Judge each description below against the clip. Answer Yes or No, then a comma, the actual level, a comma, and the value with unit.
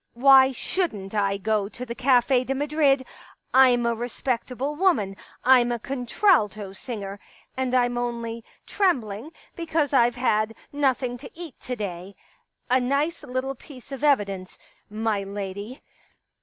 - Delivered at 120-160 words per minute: Yes, average, 145 wpm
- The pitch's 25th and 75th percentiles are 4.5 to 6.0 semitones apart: No, average, 4.1 semitones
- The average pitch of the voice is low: No, high, 245 Hz